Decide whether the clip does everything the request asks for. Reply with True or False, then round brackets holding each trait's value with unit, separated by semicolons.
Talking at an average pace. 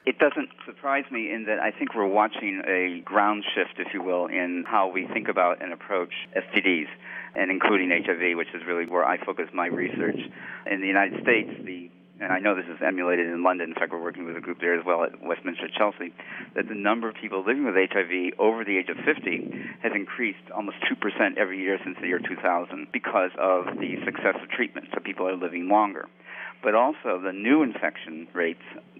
False (220 wpm)